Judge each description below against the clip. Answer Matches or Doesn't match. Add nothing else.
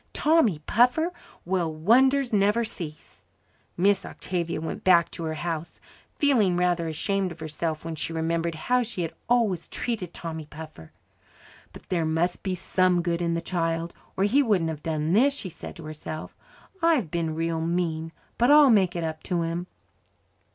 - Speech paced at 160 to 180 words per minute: Matches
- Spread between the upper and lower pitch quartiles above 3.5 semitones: Matches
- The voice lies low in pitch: Doesn't match